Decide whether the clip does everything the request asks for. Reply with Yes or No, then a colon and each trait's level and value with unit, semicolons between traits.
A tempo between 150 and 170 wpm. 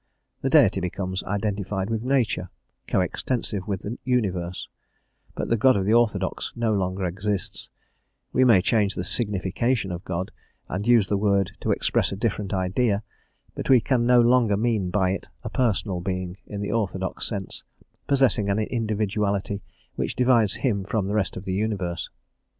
Yes: average, 165 wpm